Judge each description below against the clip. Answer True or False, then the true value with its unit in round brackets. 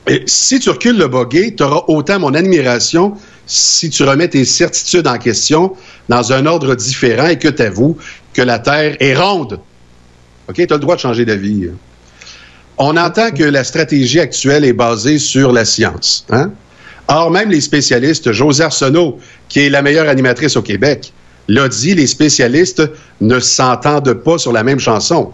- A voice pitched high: False (135 Hz)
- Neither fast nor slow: True (175 wpm)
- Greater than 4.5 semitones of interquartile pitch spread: True (5.0 semitones)